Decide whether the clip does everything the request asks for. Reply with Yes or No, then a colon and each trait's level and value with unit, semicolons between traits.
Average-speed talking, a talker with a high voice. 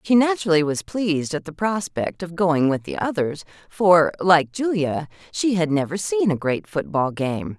No: average, 180 wpm; medium, 170 Hz